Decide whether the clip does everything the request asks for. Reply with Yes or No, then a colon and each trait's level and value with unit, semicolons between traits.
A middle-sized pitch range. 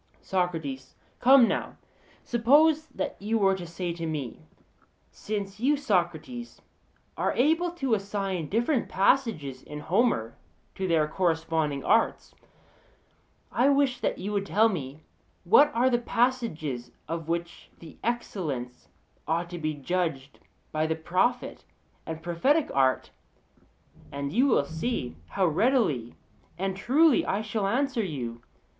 No: wide, 7.3 semitones